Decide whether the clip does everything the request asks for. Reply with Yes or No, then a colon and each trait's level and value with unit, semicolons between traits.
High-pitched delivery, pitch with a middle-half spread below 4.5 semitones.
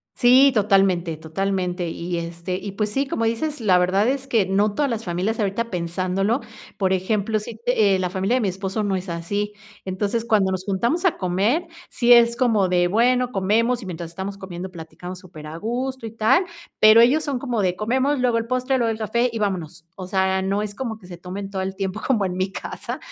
Yes: high, 200 Hz; average, 4.0 semitones